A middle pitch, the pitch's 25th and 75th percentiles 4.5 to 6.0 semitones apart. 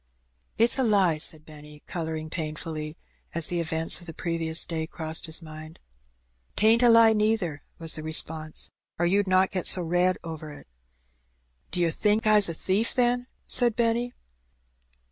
Yes: medium, 170 Hz; average, 5.0 semitones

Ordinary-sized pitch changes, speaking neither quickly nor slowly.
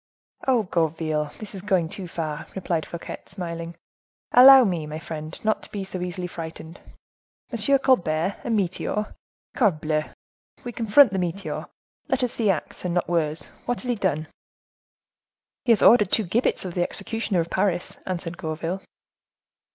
Yes: average, 4.2 semitones; average, 160 wpm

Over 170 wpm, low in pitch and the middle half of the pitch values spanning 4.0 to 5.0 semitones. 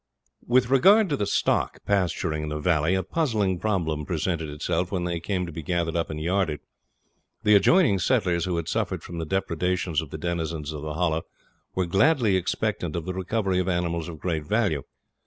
No: average, 195 wpm; very low, 90 Hz; average, 3.5 semitones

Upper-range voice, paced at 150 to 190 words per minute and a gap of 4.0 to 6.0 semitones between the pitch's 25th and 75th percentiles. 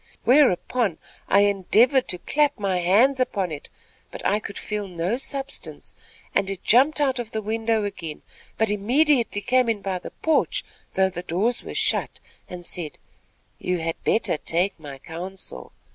Yes: high, 205 Hz; average, 165 wpm; average, 5.3 semitones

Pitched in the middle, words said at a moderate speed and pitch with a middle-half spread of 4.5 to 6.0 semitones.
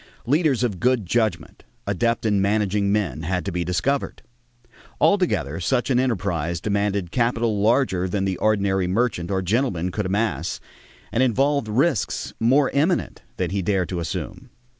No: low, 105 Hz; average, 150 wpm; average, 4.9 semitones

